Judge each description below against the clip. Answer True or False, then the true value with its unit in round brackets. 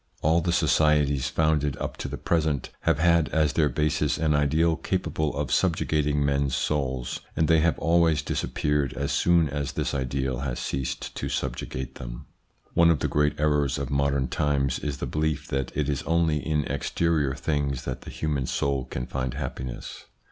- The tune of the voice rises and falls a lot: False (2.4 semitones)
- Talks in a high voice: False (75 Hz)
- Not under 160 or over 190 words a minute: True (175 wpm)